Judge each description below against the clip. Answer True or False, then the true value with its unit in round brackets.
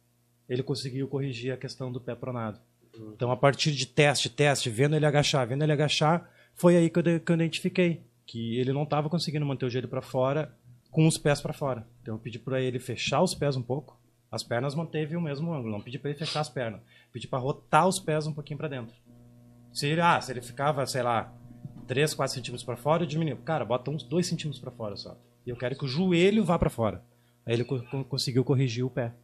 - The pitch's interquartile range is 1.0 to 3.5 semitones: False (4.0 semitones)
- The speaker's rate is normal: False (235 wpm)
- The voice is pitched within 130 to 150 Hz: True (135 Hz)